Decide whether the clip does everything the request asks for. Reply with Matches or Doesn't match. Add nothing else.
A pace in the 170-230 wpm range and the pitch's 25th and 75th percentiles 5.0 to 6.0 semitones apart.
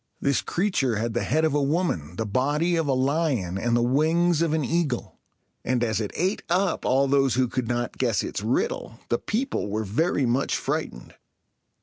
Matches